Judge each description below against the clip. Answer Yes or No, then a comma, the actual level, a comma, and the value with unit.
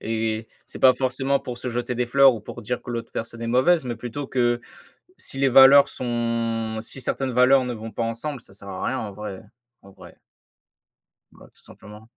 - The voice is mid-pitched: No, low, 120 Hz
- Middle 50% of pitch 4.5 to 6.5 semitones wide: No, narrow, 2.6 semitones